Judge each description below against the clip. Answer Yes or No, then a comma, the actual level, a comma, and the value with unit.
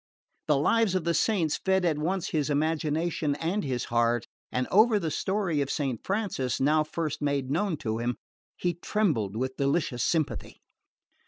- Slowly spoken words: No, average, 165 wpm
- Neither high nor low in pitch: Yes, medium, 155 Hz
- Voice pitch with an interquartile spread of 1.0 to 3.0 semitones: No, average, 4.9 semitones